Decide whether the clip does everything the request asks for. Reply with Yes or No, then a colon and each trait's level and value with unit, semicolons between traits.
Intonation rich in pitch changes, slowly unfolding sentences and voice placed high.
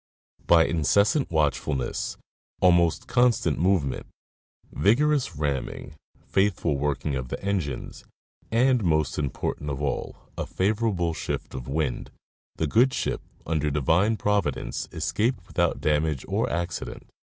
No: wide, 5.7 semitones; slow, 120 wpm; very low, 85 Hz